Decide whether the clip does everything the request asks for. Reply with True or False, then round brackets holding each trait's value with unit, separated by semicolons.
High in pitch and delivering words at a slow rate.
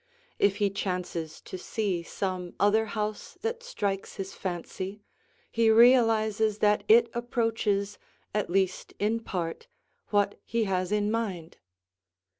True (205 Hz; 125 wpm)